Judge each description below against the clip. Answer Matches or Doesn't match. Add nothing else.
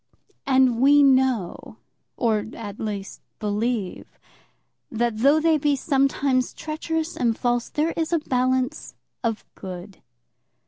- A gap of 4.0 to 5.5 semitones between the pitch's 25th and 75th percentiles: Matches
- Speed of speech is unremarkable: Doesn't match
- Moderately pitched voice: Doesn't match